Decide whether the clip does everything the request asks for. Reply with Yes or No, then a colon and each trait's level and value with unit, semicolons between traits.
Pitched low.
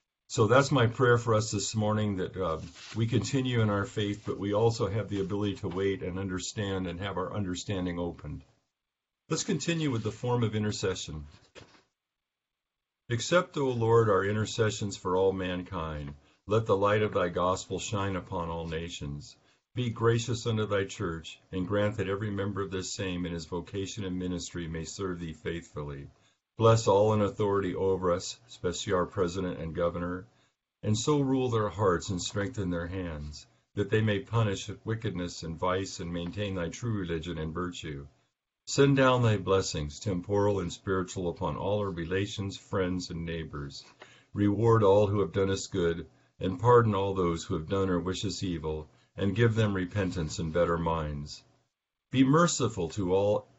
Yes: very low, 95 Hz